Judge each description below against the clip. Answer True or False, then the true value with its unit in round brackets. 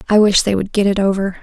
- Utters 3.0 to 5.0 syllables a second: False (6.5 syllables/s)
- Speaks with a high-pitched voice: True (200 Hz)